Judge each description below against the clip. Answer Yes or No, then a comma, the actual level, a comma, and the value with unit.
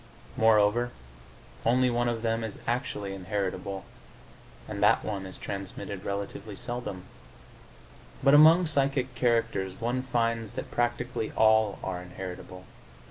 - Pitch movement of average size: Yes, average, 3.7 semitones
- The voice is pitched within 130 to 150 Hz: No, low, 110 Hz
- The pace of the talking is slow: Yes, slow, 120 wpm